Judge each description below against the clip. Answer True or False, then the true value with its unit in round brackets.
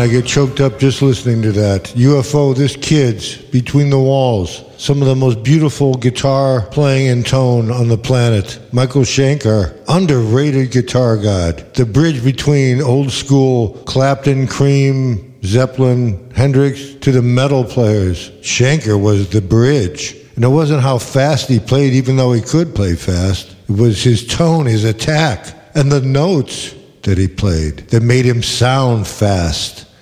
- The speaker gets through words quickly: False (155 wpm)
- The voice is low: True (125 Hz)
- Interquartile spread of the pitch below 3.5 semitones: False (3.9 semitones)